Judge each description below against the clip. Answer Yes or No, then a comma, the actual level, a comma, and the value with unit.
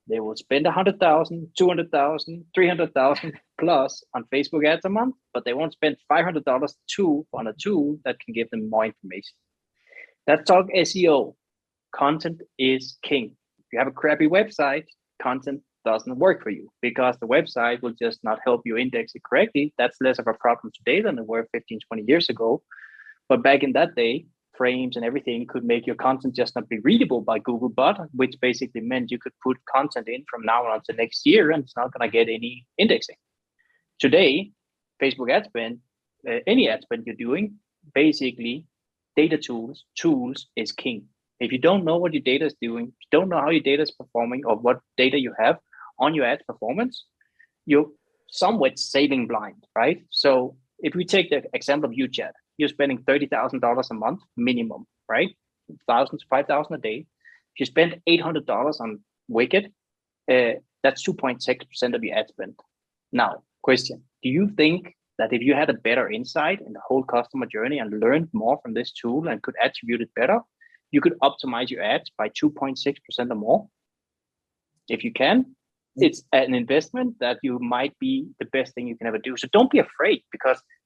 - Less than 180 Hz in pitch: Yes, medium, 140 Hz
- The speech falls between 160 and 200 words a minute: Yes, average, 195 wpm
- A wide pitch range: Yes, wide, 6.4 semitones